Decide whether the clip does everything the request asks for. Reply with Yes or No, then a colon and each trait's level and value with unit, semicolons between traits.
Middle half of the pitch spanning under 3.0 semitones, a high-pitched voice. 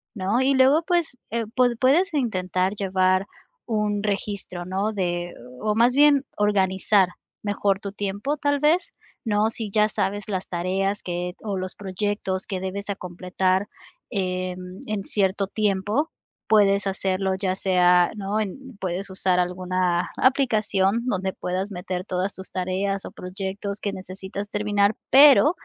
Yes: narrow, 2.4 semitones; high, 195 Hz